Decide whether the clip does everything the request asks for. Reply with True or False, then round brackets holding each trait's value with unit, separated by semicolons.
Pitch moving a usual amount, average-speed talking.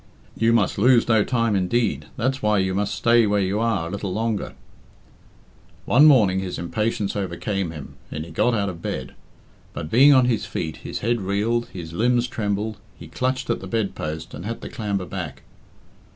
True (3.9 semitones; 190 wpm)